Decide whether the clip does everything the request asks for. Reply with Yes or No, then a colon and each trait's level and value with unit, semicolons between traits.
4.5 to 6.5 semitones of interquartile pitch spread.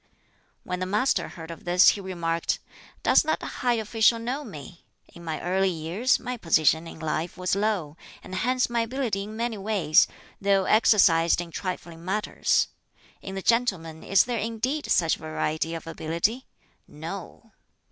Yes: average, 5.3 semitones